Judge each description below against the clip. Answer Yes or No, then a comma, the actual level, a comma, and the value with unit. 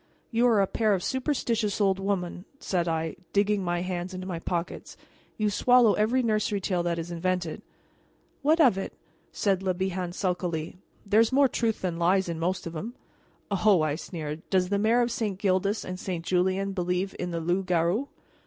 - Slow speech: No, average, 185 wpm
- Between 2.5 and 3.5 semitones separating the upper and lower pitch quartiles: Yes, average, 3.2 semitones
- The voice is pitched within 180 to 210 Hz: Yes, high, 190 Hz